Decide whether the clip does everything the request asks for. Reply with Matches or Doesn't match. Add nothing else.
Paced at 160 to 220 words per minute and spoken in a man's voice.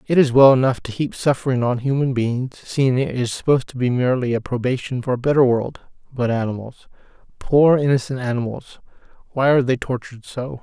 Matches